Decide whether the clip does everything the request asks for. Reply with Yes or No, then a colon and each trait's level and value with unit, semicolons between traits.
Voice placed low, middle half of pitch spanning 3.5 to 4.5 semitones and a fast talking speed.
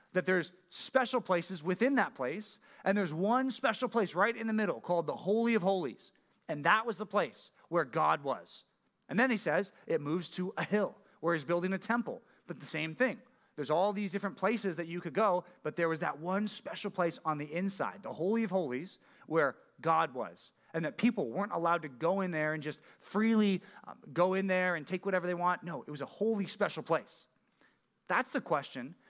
No: high, 190 Hz; average, 3.8 semitones; fast, 210 wpm